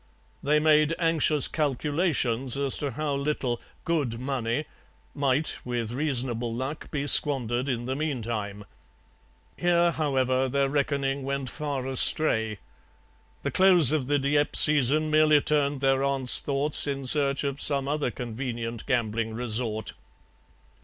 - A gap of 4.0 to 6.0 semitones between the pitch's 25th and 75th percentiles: No, average, 3.4 semitones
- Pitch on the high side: No, medium, 140 Hz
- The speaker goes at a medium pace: No, slow, 130 wpm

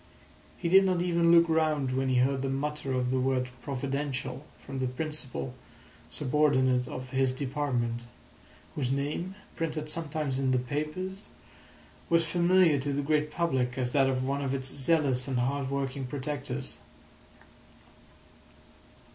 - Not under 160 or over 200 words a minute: No, average, 145 wpm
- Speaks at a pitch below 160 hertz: Yes, medium, 140 Hz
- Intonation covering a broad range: No, average, 2.9 semitones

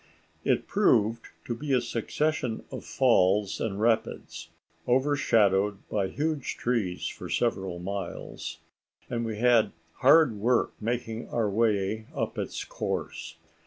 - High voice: No, low, 115 Hz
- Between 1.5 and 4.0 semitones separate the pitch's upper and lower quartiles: Yes, average, 3.4 semitones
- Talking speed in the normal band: No, slow, 125 wpm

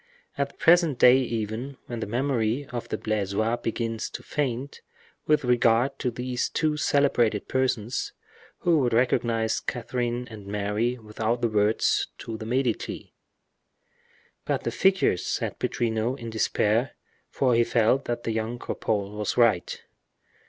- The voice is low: Yes, low, 120 Hz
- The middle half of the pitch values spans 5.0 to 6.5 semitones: No, average, 2.7 semitones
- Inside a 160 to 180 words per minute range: No, average, 145 wpm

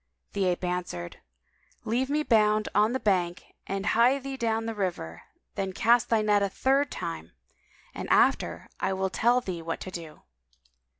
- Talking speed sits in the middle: Yes, average, 175 wpm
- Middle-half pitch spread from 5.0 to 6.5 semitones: No, average, 4.6 semitones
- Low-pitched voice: No, high, 205 Hz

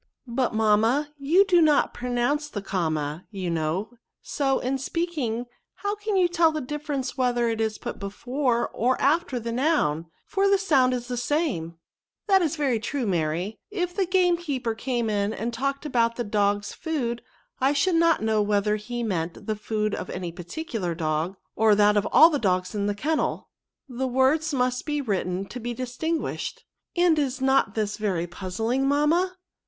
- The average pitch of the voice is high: Yes, high, 245 Hz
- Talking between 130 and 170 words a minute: No, average, 185 wpm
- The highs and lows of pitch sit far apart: Yes, wide, 6.2 semitones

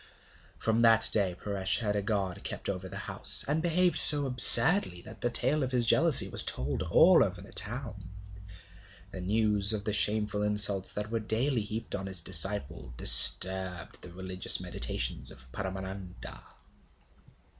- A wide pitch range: No, average, 3.4 semitones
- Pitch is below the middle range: Yes, low, 105 Hz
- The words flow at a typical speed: Yes, average, 155 wpm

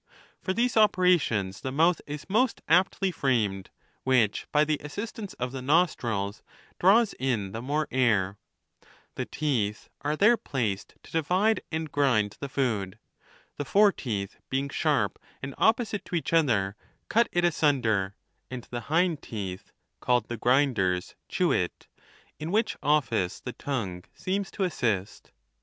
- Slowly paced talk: No, average, 150 wpm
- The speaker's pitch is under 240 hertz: Yes, low, 135 Hz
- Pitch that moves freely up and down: Yes, wide, 8.2 semitones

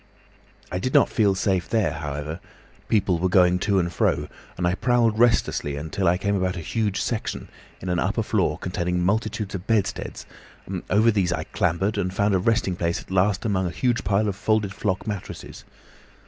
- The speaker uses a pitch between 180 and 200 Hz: No, very low, 95 Hz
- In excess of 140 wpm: Yes, average, 195 wpm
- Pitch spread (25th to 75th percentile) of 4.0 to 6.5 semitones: No, average, 3.1 semitones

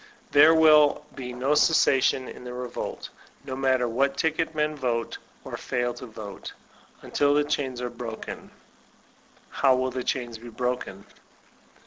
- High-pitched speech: No, low, 130 Hz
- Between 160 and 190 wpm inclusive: No, average, 150 wpm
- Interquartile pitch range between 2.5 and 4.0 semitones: Yes, average, 2.9 semitones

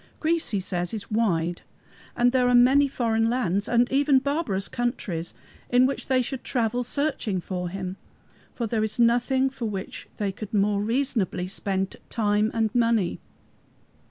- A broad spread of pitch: No, average, 4.1 semitones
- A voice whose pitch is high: Yes, high, 225 Hz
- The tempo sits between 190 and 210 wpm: No, average, 155 wpm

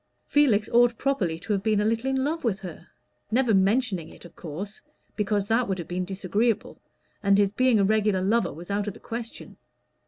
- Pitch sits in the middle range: No, high, 210 Hz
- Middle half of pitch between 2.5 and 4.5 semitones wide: Yes, average, 3.4 semitones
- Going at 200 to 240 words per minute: Yes, fast, 205 wpm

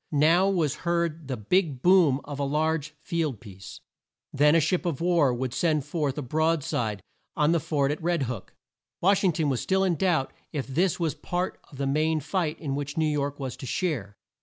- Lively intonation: No, average, 3.7 semitones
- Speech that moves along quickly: Yes, fast, 210 wpm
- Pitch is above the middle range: No, medium, 155 Hz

